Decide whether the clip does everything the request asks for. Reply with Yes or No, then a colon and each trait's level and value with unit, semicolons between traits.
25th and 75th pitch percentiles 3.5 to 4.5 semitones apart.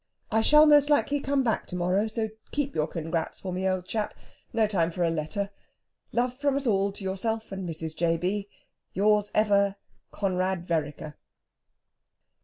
Yes: average, 4.2 semitones